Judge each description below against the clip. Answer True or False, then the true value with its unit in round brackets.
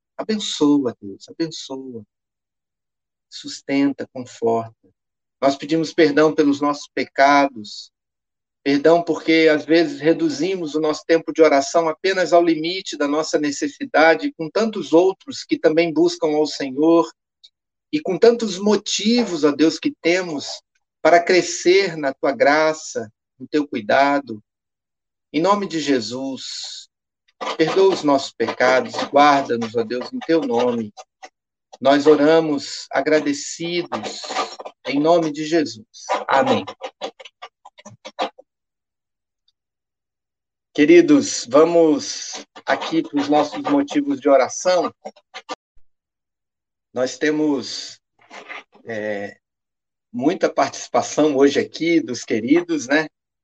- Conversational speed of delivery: False (105 wpm)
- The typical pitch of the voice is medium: True (155 Hz)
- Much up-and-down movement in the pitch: False (4.0 semitones)